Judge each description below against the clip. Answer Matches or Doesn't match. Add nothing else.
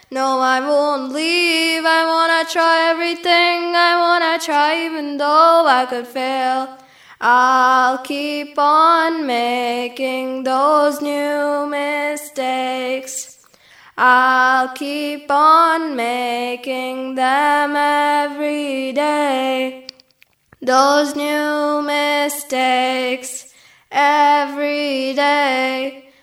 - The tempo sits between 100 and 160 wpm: Doesn't match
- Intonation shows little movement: Matches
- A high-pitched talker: Matches